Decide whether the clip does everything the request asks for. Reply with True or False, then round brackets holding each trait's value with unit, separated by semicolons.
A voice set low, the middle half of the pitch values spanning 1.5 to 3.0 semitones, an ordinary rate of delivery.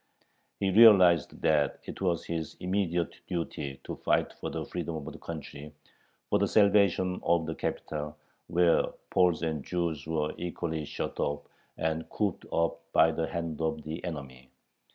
True (80 Hz; 2.4 semitones; 155 wpm)